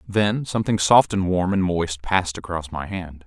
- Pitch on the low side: Yes, very low, 90 Hz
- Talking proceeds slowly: No, average, 200 wpm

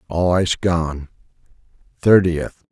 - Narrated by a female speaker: No, male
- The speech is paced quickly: No, slow, 90 wpm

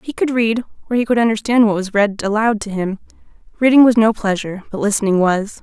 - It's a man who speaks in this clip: No, female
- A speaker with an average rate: No, fast, 215 wpm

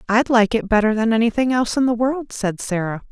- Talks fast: Yes, fast, 230 wpm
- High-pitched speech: Yes, high, 225 Hz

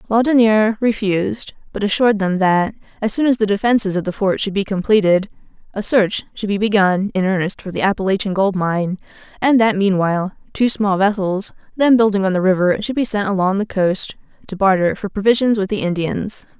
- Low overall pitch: No, high, 200 Hz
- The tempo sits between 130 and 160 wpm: No, average, 190 wpm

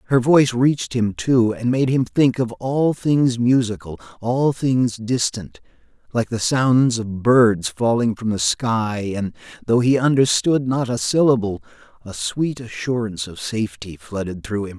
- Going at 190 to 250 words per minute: No, average, 160 wpm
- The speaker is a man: Yes, male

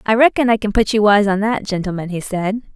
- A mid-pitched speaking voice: No, high, 210 Hz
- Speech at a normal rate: No, fast, 260 wpm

